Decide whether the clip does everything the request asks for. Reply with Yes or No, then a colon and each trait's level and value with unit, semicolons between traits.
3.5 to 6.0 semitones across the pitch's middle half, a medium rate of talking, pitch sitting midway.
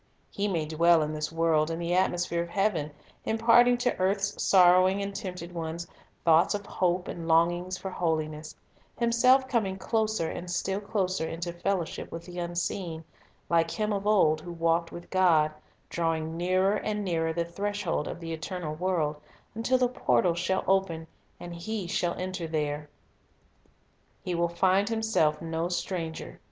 No: average, 3.1 semitones; average, 160 wpm; medium, 175 Hz